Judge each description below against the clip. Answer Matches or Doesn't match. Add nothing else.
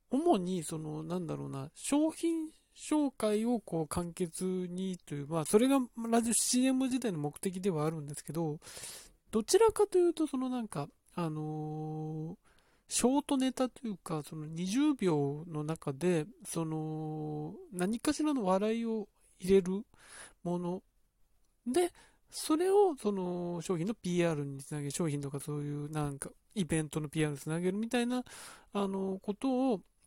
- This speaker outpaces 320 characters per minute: Doesn't match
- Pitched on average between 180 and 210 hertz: Matches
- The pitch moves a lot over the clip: Matches